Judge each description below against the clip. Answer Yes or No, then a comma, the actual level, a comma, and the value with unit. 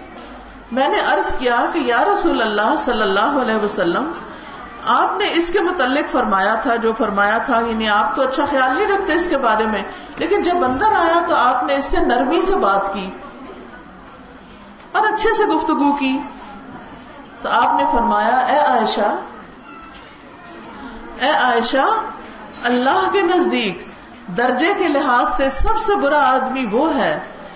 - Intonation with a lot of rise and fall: Yes, wide, 7.1 semitones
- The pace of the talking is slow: No, average, 155 wpm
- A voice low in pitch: No, very high, 270 Hz